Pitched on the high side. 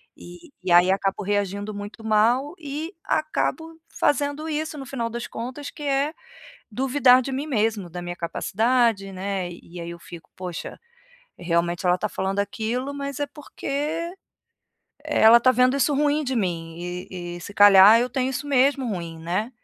Yes: high, 230 Hz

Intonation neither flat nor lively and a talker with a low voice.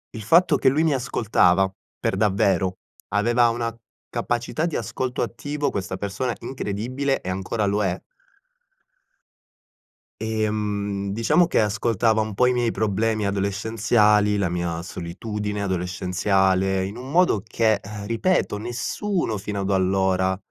Yes: average, 3.6 semitones; low, 105 Hz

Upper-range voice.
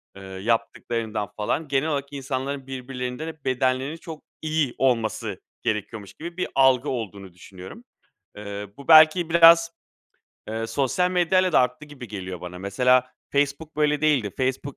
No: low, 130 Hz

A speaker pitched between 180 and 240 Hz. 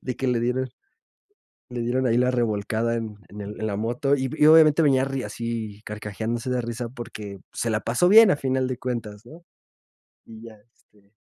No: low, 120 Hz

